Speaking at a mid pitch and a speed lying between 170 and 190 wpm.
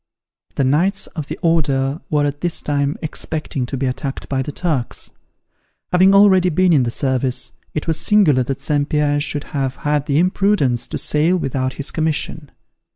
Yes: medium, 145 Hz; average, 175 wpm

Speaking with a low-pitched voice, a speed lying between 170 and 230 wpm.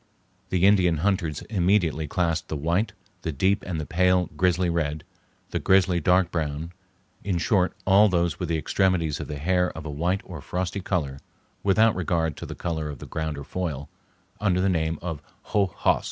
Yes: very low, 90 Hz; average, 180 wpm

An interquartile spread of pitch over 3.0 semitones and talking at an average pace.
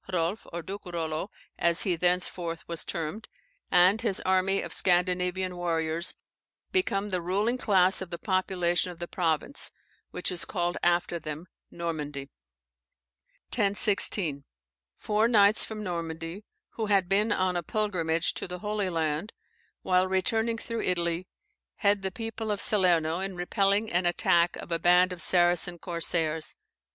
No: average, 2.7 semitones; average, 145 wpm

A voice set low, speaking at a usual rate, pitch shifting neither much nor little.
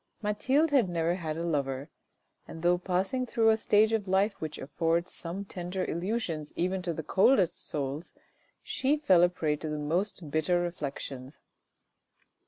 No: medium, 175 Hz; average, 160 wpm; average, 4.2 semitones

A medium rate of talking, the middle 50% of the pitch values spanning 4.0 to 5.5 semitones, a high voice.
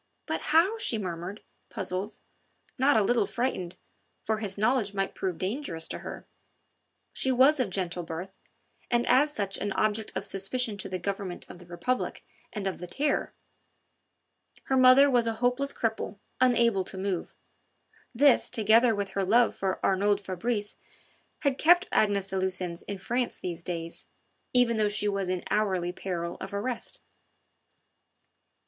Yes: average, 155 wpm; average, 4.5 semitones; high, 205 Hz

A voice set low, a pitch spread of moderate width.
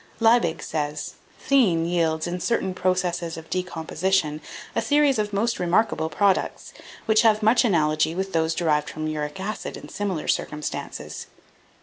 No: medium, 175 Hz; average, 4.6 semitones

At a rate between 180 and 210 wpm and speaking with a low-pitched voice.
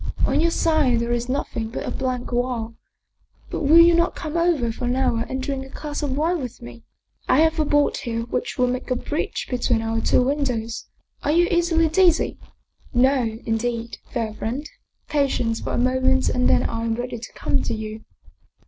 No: average, 200 wpm; very high, 255 Hz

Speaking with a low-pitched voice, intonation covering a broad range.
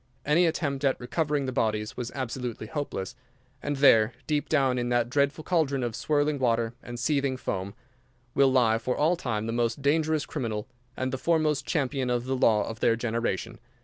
No: low, 130 Hz; average, 3.8 semitones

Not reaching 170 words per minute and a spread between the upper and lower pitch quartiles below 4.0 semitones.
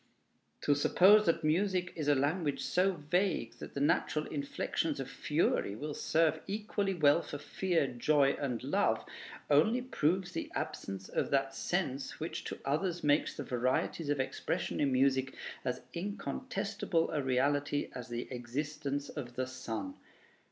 No: average, 150 wpm; average, 4.8 semitones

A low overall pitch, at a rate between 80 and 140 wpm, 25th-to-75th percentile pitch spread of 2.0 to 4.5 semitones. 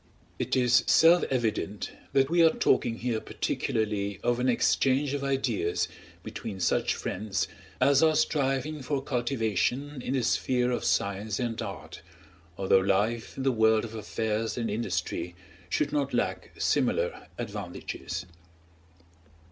Yes: low, 120 Hz; slow, 135 wpm; average, 4.2 semitones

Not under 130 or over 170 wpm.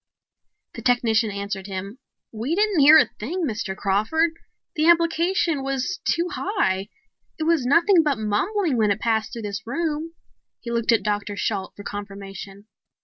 Yes: average, 155 wpm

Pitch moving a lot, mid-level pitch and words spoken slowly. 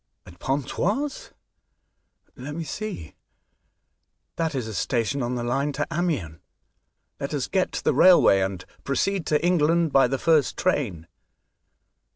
No: wide, 5.9 semitones; medium, 145 Hz; average, 145 wpm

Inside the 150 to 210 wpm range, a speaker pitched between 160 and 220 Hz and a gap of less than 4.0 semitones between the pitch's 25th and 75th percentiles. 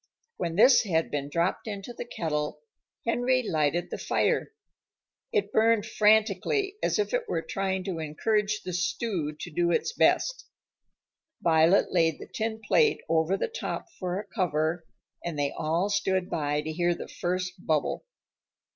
No: average, 155 wpm; medium, 185 Hz; average, 5.2 semitones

